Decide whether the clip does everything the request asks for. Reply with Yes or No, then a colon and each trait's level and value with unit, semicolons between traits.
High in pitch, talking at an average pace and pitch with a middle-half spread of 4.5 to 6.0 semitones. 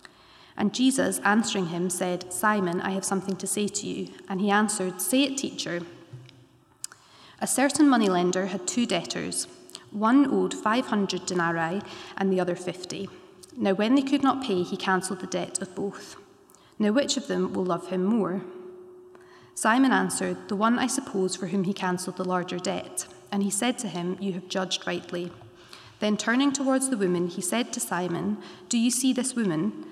Yes: high, 195 Hz; average, 180 wpm; average, 4.8 semitones